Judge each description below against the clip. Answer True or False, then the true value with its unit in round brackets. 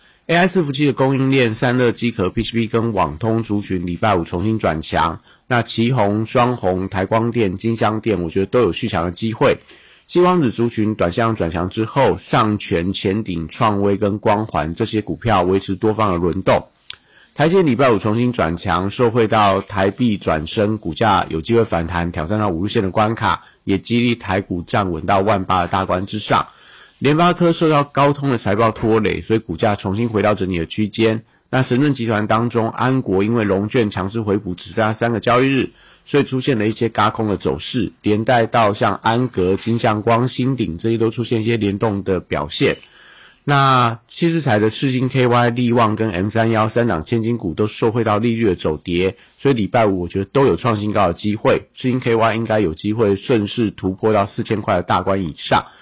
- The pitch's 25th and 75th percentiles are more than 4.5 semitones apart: False (3.5 semitones)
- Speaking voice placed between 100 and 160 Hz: True (110 Hz)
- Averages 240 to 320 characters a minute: True (300 characters per minute)